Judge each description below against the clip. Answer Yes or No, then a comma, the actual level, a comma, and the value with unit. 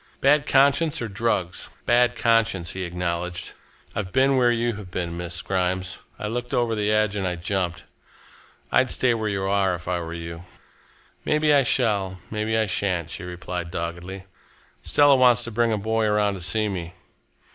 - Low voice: Yes, low, 100 Hz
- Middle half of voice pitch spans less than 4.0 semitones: No, average, 4.8 semitones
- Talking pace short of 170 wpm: No, average, 185 wpm